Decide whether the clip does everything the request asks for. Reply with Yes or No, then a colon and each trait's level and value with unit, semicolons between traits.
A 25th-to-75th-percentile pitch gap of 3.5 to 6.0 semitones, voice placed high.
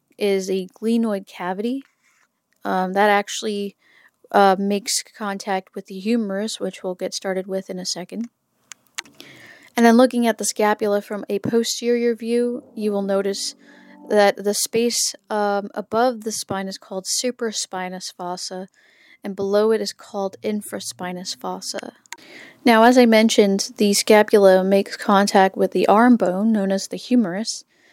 No: average, 3.1 semitones; high, 205 Hz